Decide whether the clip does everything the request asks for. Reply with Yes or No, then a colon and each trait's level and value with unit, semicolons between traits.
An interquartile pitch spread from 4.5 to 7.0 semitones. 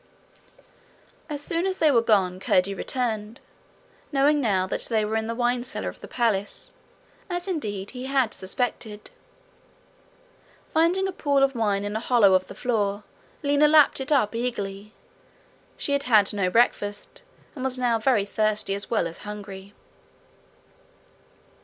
Yes: average, 4.9 semitones